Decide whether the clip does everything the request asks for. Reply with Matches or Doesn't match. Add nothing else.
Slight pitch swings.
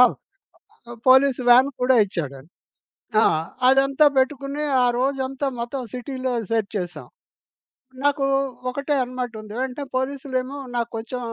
Matches